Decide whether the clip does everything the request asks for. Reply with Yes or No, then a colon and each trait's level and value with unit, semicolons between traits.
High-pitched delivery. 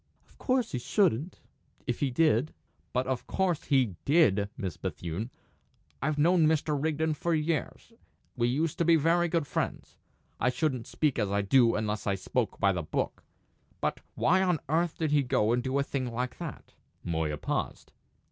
No: medium, 140 Hz